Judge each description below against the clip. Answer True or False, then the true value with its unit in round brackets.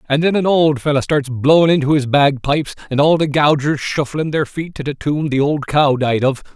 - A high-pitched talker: False (145 Hz)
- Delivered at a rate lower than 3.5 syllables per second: False (5.3 syllables/s)